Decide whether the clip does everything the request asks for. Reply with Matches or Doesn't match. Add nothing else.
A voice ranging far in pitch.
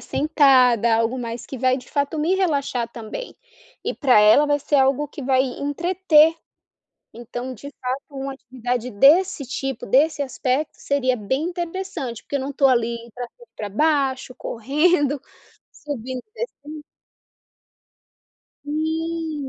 Doesn't match